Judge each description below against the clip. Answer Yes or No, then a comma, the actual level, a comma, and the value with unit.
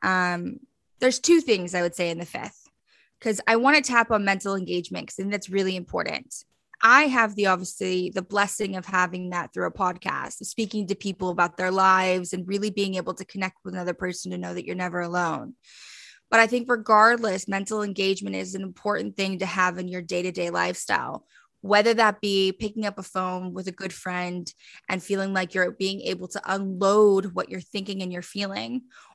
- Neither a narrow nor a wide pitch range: No, narrow, 2.2 semitones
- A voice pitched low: No, high, 190 Hz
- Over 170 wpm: Yes, average, 200 wpm